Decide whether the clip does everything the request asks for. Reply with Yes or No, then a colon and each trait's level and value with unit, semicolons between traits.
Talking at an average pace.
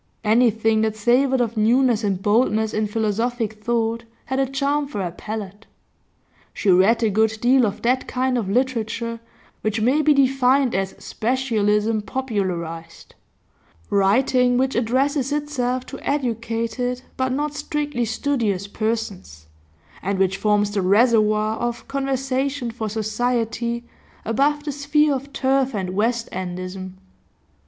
No: slow, 130 wpm